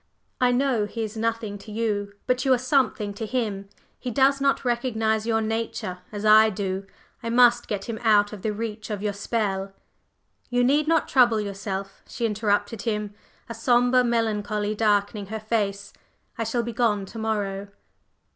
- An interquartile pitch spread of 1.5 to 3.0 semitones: Yes, narrow, 2.5 semitones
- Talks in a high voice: Yes, high, 220 Hz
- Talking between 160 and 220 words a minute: Yes, average, 175 wpm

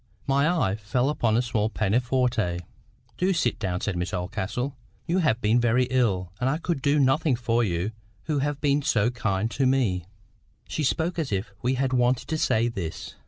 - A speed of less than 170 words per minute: No, average, 185 wpm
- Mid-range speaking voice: No, low, 120 Hz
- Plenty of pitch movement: No, average, 4.5 semitones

